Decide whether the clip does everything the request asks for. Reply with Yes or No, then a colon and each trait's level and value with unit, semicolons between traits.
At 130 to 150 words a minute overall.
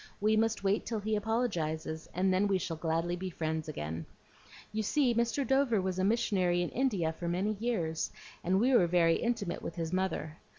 No: average, 195 wpm